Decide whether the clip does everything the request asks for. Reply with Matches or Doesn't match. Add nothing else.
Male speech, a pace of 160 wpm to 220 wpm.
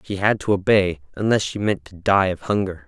Doesn't match